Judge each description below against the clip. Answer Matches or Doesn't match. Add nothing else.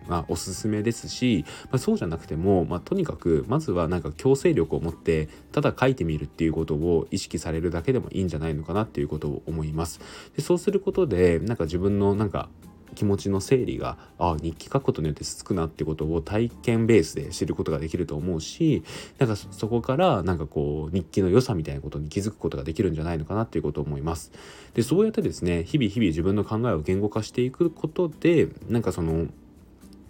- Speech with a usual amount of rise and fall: Doesn't match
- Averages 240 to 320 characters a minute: Doesn't match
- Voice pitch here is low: Matches